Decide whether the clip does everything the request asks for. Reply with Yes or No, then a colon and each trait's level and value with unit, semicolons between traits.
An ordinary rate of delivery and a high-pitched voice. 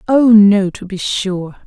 Yes: average, 180 wpm; high, 200 Hz